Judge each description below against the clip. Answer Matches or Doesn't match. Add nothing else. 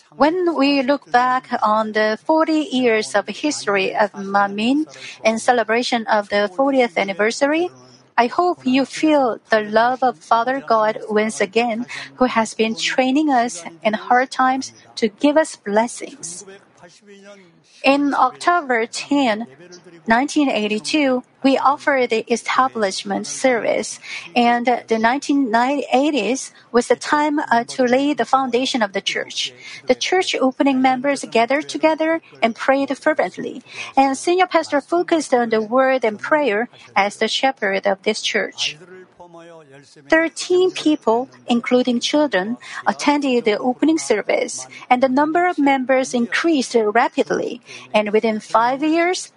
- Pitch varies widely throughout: Doesn't match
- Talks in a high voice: Matches